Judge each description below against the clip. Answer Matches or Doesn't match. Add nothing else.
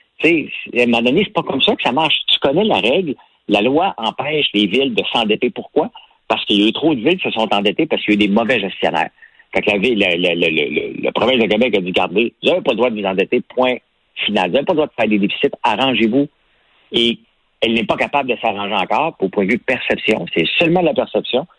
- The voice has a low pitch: Matches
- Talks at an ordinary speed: Doesn't match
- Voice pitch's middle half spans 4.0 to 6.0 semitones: Matches